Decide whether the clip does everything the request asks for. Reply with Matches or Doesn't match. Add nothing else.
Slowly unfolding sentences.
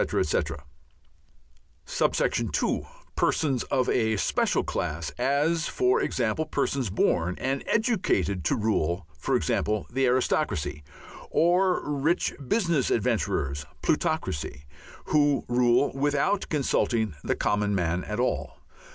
Matches